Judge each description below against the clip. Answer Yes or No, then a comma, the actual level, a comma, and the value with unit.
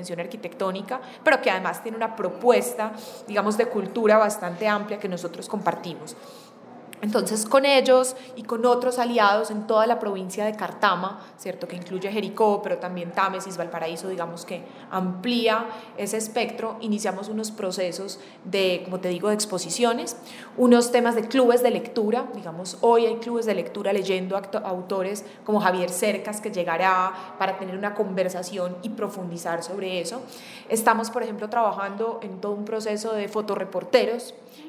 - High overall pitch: Yes, high, 210 Hz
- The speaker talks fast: No, average, 150 wpm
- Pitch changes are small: No, average, 3.7 semitones